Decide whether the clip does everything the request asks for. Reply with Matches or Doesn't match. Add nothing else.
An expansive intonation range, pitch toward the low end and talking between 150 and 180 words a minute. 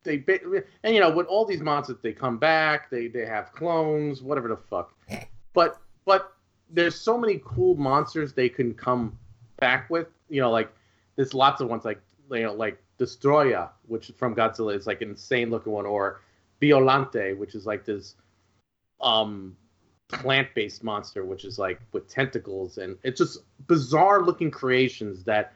Matches